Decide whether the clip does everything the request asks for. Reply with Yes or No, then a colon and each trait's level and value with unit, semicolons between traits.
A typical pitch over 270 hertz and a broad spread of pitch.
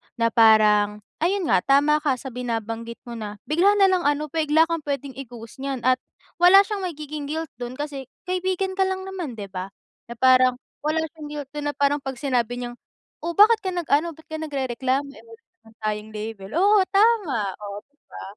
Yes: very high, 285 Hz; wide, 6.0 semitones